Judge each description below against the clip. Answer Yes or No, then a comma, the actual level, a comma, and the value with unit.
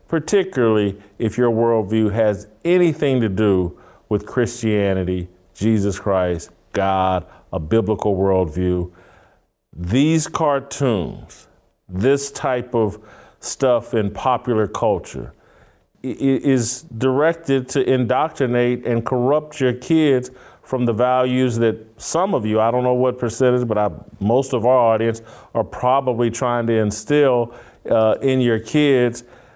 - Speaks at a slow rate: Yes, slow, 120 wpm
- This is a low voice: Yes, low, 115 Hz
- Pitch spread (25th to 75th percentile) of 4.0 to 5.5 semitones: No, average, 3.6 semitones